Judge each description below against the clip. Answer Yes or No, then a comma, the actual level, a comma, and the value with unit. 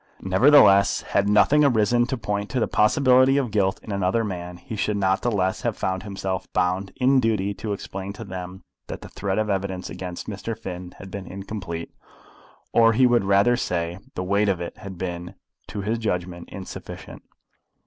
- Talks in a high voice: No, low, 100 Hz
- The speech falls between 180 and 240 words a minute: Yes, average, 190 wpm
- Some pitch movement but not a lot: Yes, average, 3.1 semitones